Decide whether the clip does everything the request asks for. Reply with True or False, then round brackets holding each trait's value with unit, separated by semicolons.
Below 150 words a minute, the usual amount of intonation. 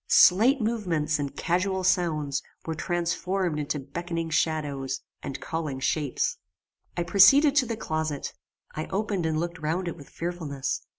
True (140 wpm; 3.5 semitones)